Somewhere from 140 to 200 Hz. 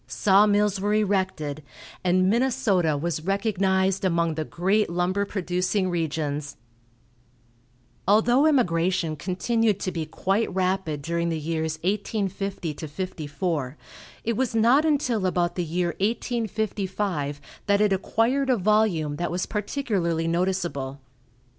Yes: medium, 185 Hz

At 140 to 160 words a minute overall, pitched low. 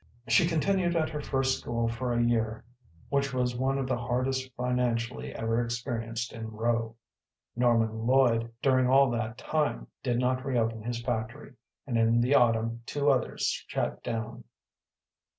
Yes: average, 150 wpm; low, 120 Hz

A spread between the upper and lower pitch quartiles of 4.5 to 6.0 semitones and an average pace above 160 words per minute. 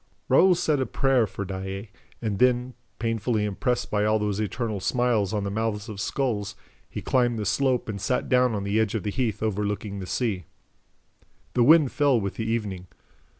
No: average, 3.5 semitones; average, 190 wpm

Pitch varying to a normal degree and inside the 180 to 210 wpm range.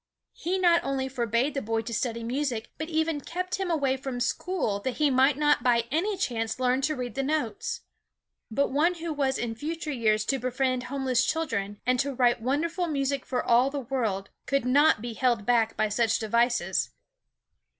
Yes: average, 4.1 semitones; average, 190 wpm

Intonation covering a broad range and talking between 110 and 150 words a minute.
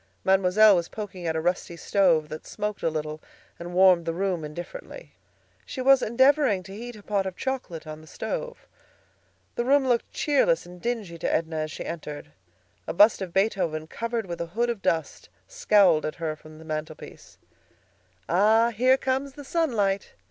No: wide, 6.3 semitones; average, 175 wpm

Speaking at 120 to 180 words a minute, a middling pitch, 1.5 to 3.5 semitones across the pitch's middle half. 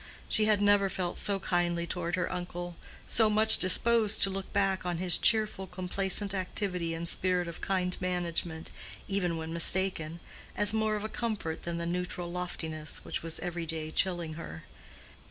Yes: average, 170 wpm; medium, 180 Hz; narrow, 2.6 semitones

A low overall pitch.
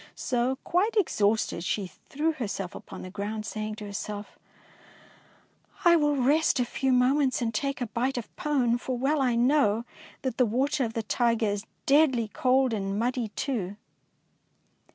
No: high, 245 Hz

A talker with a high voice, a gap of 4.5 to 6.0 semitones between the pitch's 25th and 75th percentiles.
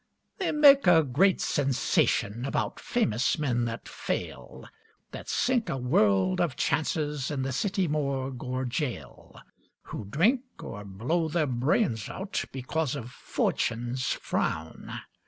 No: low, 135 Hz; average, 5.3 semitones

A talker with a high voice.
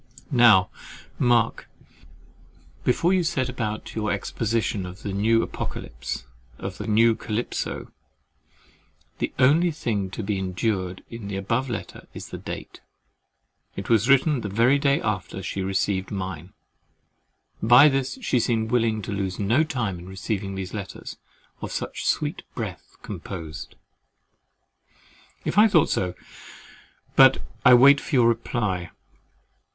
No: low, 110 Hz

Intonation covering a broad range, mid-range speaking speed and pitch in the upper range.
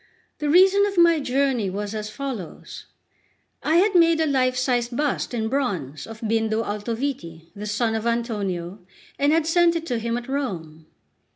Yes: wide, 5.7 semitones; average, 170 wpm; high, 240 Hz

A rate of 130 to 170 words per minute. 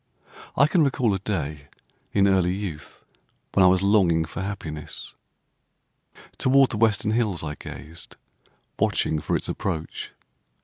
Yes: slow, 135 wpm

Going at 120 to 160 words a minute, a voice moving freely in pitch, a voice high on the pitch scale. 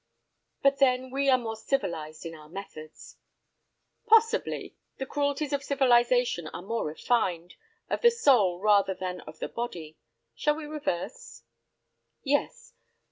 Yes: slow, 135 wpm; wide, 8.1 semitones; high, 245 Hz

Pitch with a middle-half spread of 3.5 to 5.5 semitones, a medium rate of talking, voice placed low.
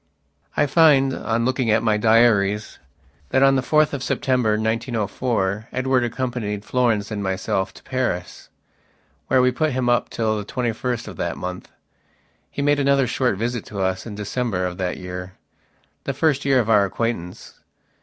Yes: average, 3.9 semitones; average, 165 wpm; low, 115 Hz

